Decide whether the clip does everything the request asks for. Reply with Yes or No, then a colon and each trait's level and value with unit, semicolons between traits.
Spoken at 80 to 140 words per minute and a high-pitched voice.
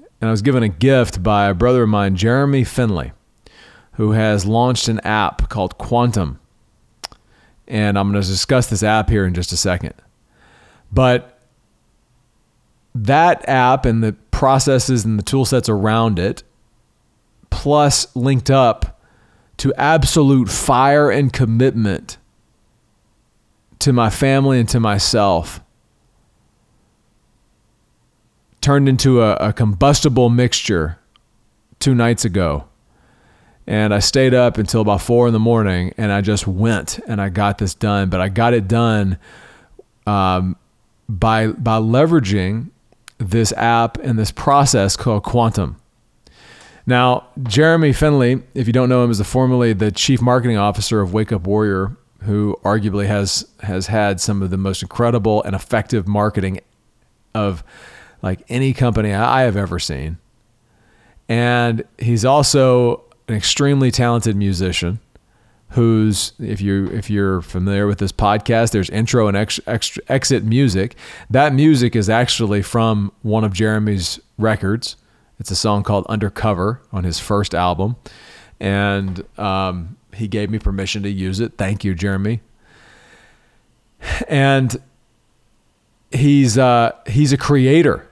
No: slow, 135 wpm; low, 110 Hz